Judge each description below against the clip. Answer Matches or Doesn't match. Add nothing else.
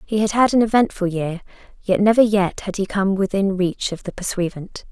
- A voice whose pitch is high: Matches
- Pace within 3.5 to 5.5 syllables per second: Matches